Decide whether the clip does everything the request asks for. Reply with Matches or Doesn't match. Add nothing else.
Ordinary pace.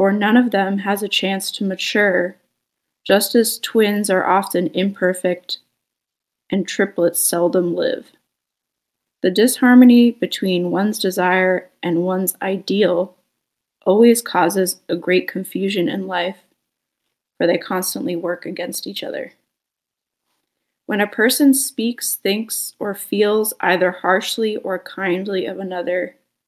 Doesn't match